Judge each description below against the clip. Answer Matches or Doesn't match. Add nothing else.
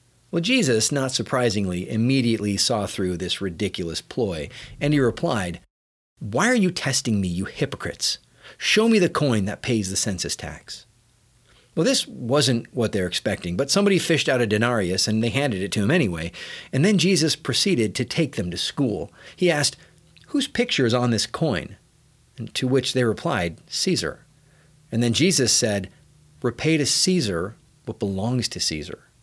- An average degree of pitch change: Doesn't match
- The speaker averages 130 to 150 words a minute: Doesn't match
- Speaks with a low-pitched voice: Matches